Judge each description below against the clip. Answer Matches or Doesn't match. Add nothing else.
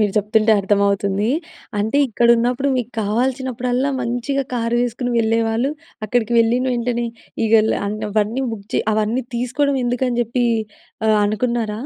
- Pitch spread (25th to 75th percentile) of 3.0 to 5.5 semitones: Doesn't match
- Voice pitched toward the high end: Matches